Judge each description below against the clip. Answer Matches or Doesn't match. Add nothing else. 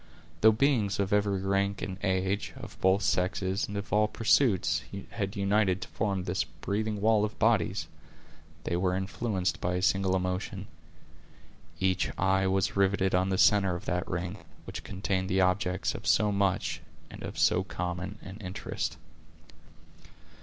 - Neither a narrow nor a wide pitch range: Doesn't match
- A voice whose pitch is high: Doesn't match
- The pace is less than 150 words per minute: Doesn't match